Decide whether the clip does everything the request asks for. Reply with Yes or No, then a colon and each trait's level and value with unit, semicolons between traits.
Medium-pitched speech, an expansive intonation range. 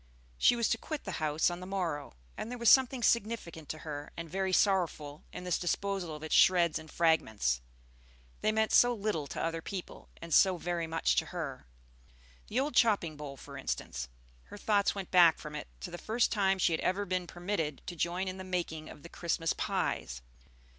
No: medium, 175 Hz; average, 4.0 semitones